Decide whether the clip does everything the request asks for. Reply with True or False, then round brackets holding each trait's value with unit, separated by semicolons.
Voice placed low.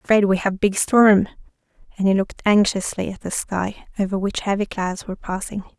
False (200 Hz)